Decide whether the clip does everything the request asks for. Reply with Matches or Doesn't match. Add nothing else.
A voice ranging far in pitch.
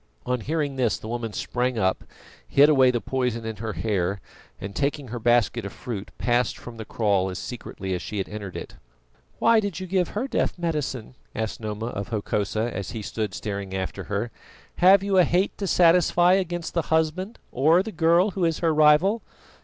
Matches